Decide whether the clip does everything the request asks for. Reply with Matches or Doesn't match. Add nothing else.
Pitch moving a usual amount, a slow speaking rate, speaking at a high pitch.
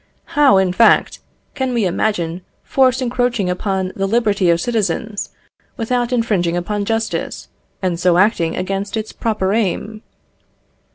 Matches